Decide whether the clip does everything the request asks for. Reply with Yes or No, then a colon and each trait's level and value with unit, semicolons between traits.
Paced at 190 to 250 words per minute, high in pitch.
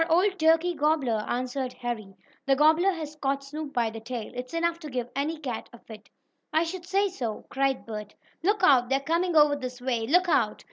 Yes: fast, 205 wpm; very high, 280 Hz